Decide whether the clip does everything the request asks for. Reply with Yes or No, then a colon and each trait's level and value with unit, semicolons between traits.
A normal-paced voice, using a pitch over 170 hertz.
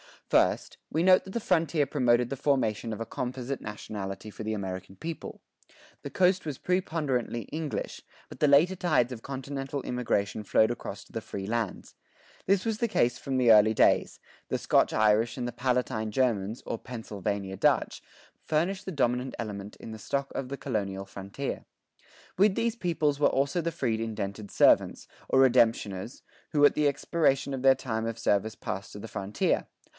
No: average, 180 wpm; low, 125 Hz